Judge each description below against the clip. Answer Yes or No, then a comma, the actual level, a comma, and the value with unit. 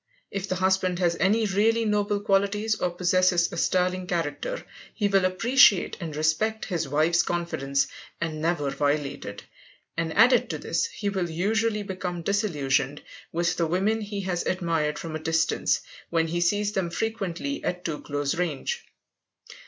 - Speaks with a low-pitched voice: No, medium, 180 Hz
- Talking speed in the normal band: Yes, average, 160 wpm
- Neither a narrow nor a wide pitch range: Yes, average, 3.8 semitones